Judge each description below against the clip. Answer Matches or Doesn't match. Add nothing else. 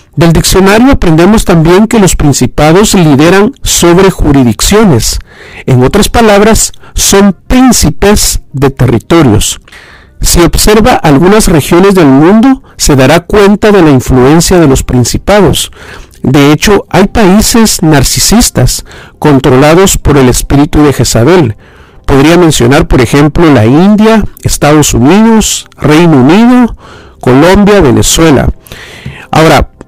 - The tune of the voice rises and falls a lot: Matches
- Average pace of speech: Doesn't match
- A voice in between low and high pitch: Matches